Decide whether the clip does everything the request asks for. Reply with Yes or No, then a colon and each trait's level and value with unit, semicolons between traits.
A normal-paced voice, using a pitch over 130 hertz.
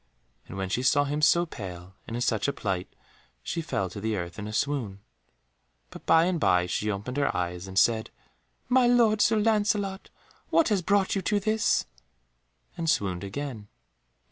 Yes: average, 180 wpm; medium, 140 Hz